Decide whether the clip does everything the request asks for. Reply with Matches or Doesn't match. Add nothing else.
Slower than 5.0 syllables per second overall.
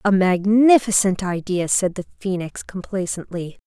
Matches